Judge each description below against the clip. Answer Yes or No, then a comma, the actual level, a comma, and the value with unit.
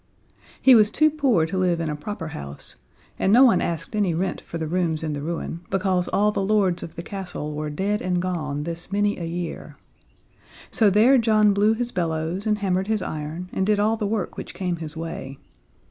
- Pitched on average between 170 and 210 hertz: Yes, medium, 185 Hz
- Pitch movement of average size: Yes, average, 4.2 semitones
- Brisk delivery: Yes, fast, 210 wpm